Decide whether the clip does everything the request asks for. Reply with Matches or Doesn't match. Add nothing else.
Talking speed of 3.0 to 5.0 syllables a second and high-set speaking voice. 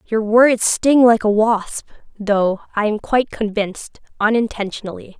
Matches